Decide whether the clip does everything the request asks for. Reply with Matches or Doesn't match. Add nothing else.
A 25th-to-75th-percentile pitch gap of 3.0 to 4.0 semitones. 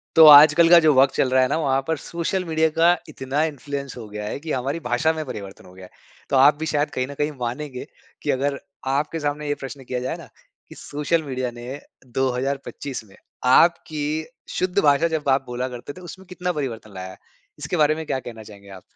Matches